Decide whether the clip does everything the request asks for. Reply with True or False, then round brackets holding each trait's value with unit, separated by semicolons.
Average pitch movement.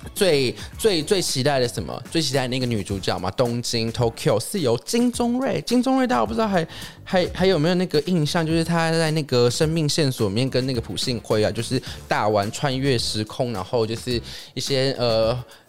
False (6.3 semitones)